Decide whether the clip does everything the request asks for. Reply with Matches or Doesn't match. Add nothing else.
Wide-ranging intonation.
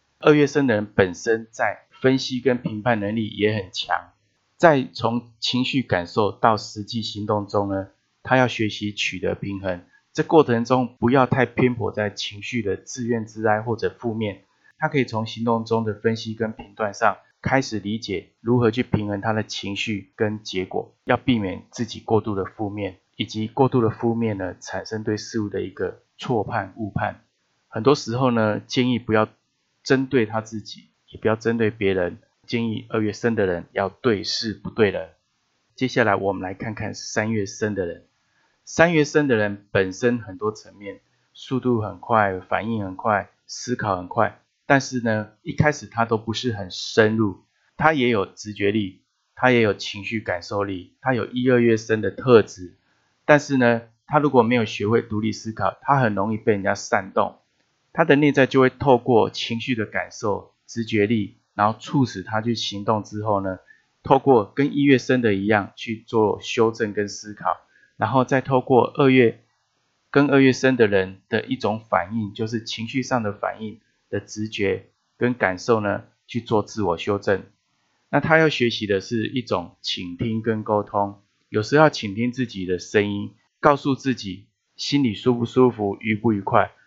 Doesn't match